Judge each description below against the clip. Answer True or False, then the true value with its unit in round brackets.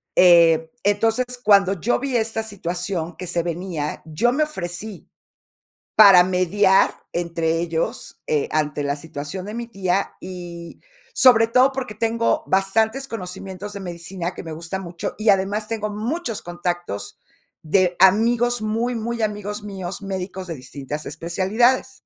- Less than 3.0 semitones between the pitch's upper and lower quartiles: False (4.3 semitones)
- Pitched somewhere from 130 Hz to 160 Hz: False (190 Hz)